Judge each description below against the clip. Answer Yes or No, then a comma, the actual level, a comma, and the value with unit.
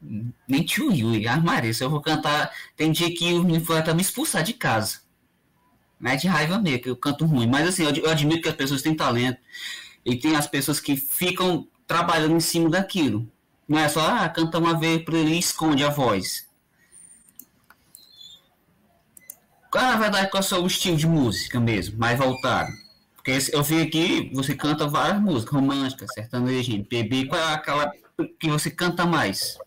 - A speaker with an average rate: No, fast, 190 wpm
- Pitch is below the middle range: No, medium, 155 Hz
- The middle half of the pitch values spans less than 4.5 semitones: Yes, average, 4.1 semitones